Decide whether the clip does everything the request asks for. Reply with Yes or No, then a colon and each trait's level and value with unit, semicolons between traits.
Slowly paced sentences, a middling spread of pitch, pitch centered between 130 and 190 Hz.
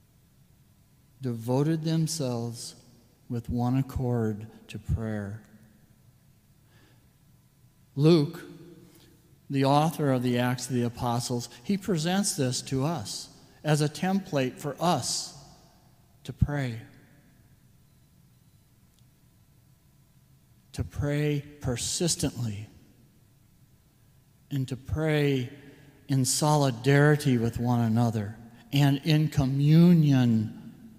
Yes: slow, 80 wpm; average, 3.3 semitones; low, 135 Hz